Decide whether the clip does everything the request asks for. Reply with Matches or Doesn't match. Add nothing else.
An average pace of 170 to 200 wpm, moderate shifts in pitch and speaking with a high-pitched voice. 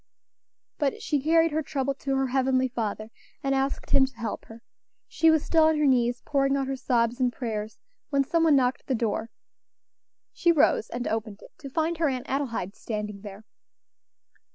Matches